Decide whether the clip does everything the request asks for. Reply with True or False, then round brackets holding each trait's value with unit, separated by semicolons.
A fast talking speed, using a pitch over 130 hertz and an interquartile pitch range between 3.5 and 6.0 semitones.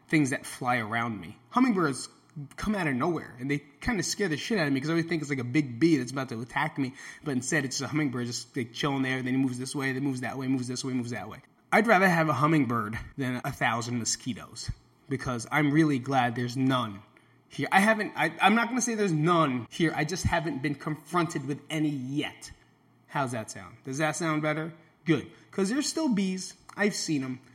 True (235 wpm; 140 Hz; 4.2 semitones)